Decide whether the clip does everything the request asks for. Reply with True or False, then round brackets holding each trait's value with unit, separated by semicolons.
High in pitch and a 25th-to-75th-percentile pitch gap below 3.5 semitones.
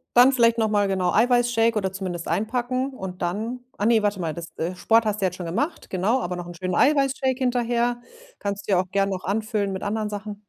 False (210 Hz; 4.2 semitones)